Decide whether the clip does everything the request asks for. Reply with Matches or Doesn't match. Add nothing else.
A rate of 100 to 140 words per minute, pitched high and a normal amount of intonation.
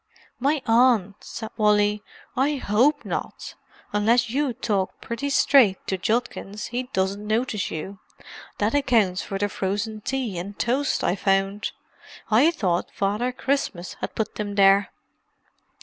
Matches